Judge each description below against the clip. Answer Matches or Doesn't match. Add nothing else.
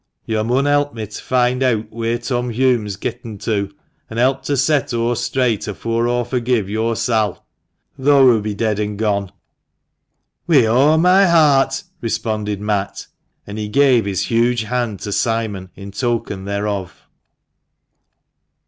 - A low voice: Matches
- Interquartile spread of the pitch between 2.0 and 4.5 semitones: Matches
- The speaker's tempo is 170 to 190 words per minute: Doesn't match